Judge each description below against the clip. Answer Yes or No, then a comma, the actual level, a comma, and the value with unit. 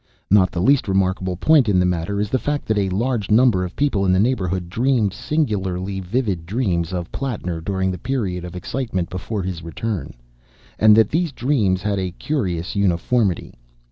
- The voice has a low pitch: Yes, very low, 95 Hz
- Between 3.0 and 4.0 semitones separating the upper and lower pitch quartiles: No, average, 4.6 semitones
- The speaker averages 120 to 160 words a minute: No, average, 180 wpm